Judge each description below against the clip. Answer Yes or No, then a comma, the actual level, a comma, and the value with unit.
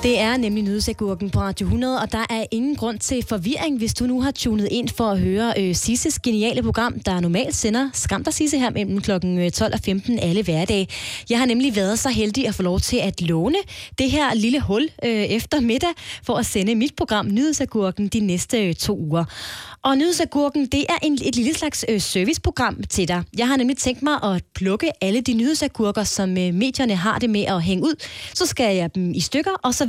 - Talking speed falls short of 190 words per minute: No, average, 220 wpm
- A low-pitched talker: No, high, 230 Hz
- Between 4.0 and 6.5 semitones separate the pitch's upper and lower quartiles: Yes, wide, 5.4 semitones